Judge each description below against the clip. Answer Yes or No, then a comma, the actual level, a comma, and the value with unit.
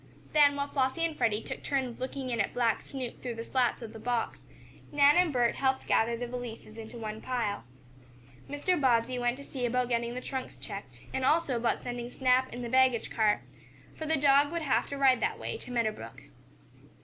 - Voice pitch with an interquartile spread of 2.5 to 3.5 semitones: Yes, average, 2.9 semitones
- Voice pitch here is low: No, very high, 250 Hz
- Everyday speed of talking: No, fast, 210 wpm